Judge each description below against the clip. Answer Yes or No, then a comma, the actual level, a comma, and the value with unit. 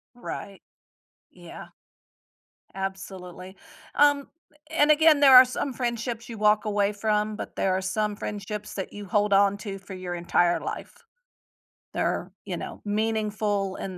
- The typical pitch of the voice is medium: No, high, 210 Hz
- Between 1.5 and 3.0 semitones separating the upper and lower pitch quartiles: Yes, narrow, 2.6 semitones